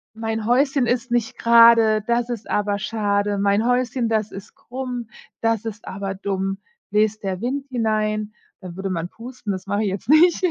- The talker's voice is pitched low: No, high, 220 Hz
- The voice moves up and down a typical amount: Yes, average, 3.0 semitones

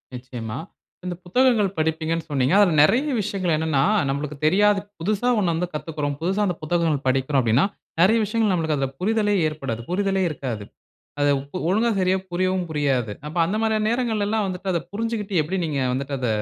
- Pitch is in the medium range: Yes, medium, 170 Hz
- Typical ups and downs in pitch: No, wide, 5.9 semitones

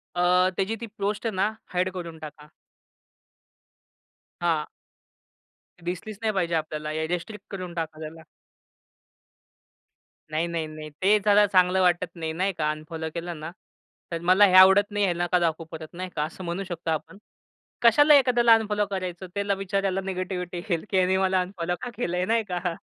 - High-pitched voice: No, medium, 180 Hz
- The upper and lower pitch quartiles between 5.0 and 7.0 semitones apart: No, average, 2.9 semitones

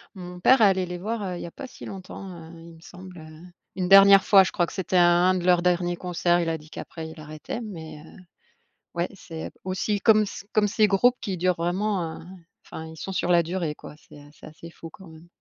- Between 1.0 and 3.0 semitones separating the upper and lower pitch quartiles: Yes, average, 2.7 semitones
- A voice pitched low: No, medium, 180 Hz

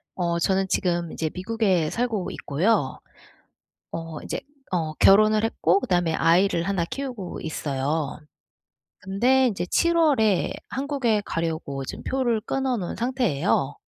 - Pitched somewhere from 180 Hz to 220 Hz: Yes, high, 190 Hz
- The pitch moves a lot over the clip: Yes, wide, 5.7 semitones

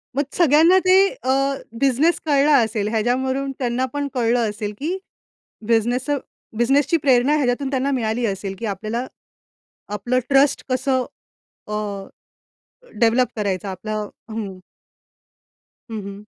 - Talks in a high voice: Yes, high, 245 Hz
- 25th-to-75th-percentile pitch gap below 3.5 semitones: No, average, 4.1 semitones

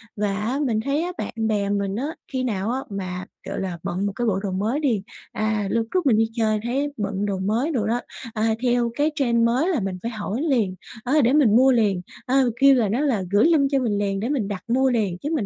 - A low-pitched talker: No, high, 225 Hz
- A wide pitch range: No, average, 4.6 semitones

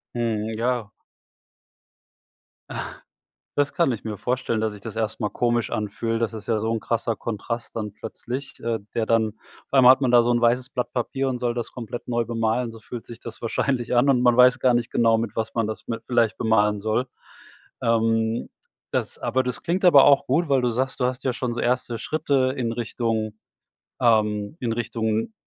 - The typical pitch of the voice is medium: No, low, 115 Hz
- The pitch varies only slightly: Yes, narrow, 2.1 semitones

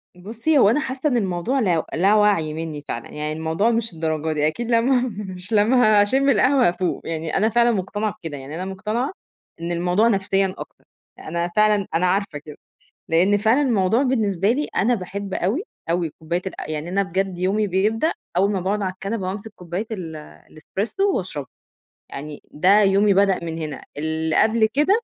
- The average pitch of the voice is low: No, high, 195 Hz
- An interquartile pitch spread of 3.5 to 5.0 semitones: Yes, average, 4.6 semitones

